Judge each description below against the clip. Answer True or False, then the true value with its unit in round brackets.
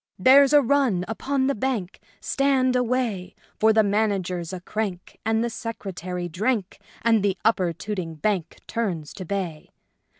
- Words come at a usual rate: True (160 wpm)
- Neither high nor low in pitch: False (210 Hz)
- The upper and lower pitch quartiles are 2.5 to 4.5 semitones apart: False (5.0 semitones)